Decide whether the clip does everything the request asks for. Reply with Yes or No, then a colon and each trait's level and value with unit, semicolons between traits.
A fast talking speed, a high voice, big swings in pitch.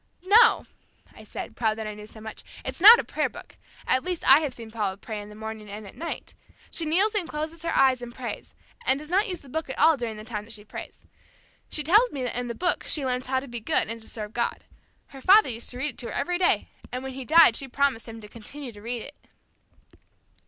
Yes: fast, 260 wpm; very high, 255 Hz; wide, 5.9 semitones